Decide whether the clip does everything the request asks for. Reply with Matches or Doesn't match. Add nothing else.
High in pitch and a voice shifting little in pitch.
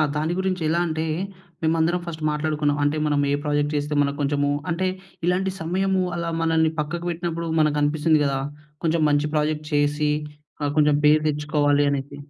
Doesn't match